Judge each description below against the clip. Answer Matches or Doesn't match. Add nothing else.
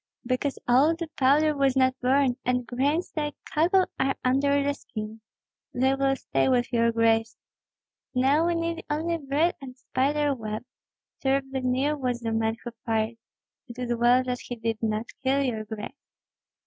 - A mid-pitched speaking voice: Doesn't match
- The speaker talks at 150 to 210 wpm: Matches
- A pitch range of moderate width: Matches